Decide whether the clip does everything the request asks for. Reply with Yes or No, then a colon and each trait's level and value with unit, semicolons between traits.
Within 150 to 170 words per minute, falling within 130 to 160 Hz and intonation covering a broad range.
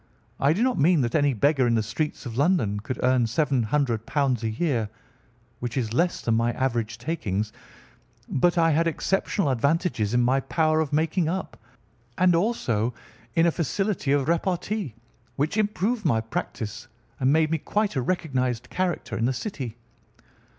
Yes: average, 160 wpm; medium, 140 Hz; wide, 6.0 semitones